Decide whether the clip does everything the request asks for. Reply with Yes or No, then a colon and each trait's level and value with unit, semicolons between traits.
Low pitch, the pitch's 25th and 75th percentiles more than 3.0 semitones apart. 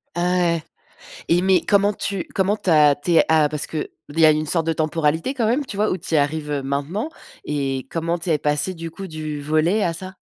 No: medium, 165 Hz; average, 3.7 semitones